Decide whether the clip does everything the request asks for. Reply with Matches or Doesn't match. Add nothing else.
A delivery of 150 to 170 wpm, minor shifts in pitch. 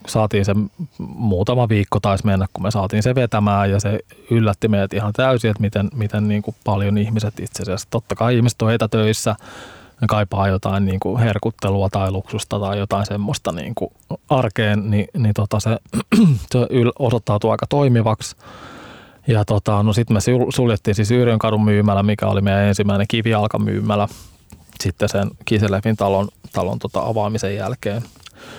Matches